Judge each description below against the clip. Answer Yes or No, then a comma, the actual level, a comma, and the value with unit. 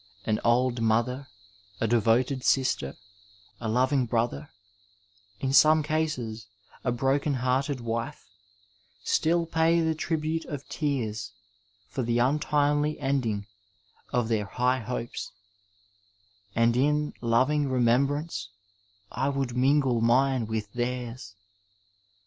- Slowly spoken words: Yes, slow, 110 wpm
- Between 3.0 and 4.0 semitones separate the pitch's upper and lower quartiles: Yes, average, 3.7 semitones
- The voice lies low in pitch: Yes, low, 125 Hz